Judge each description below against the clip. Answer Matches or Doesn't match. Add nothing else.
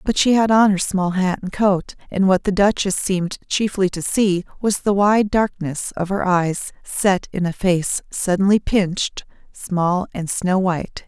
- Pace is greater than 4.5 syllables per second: Doesn't match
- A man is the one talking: Doesn't match